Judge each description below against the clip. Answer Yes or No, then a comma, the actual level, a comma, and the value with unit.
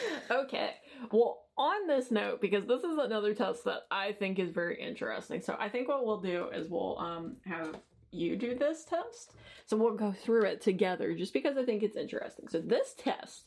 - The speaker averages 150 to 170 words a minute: No, average, 200 wpm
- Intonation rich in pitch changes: Yes, wide, 5.8 semitones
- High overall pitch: Yes, high, 230 Hz